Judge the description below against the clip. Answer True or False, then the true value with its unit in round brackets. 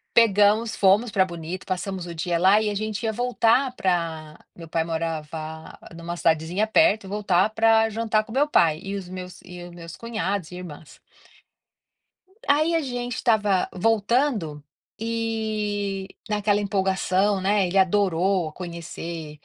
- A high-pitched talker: True (195 Hz)